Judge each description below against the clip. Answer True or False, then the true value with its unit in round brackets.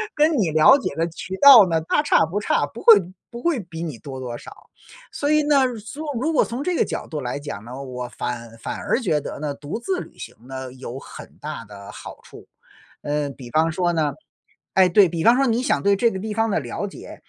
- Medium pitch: True (165 Hz)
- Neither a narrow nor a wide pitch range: False (8.8 semitones)